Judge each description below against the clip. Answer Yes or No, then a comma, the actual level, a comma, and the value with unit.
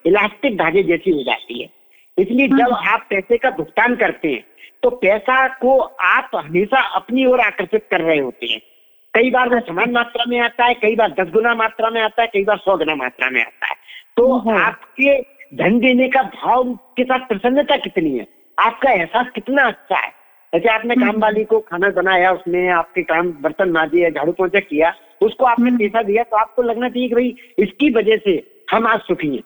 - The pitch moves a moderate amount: Yes, average, 4.6 semitones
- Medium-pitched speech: No, high, 225 Hz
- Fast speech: Yes, fast, 200 wpm